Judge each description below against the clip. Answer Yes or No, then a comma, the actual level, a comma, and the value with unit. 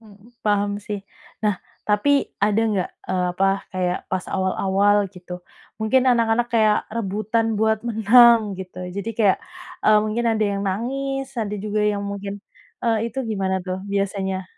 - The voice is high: Yes, high, 210 Hz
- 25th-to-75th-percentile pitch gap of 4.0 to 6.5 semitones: No, narrow, 2.4 semitones